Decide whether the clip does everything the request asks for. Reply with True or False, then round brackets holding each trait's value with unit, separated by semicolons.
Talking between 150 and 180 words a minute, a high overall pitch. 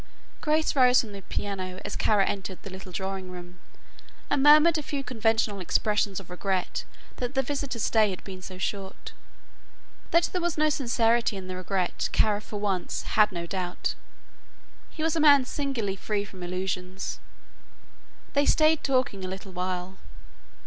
True (165 wpm; 205 Hz)